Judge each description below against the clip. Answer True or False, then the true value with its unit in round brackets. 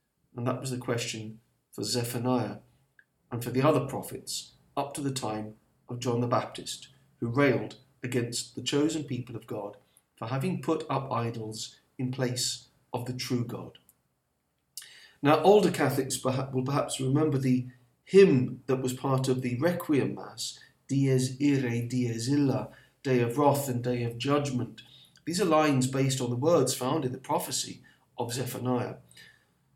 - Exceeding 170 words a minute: False (160 wpm)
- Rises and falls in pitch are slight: True (2.1 semitones)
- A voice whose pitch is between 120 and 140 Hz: True (130 Hz)